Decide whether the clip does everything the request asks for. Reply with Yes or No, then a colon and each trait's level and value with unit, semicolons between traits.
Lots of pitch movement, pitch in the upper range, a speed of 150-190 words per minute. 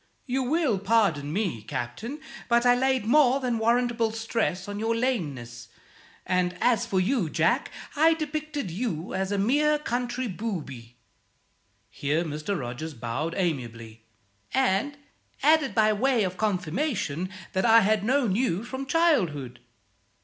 No: wide, 7.6 semitones; high, 215 Hz; slow, 135 wpm